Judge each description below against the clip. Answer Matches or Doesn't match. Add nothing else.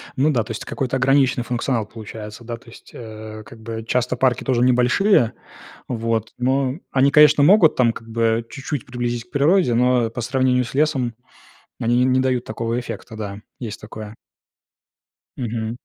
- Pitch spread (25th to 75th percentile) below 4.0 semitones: Matches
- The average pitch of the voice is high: Doesn't match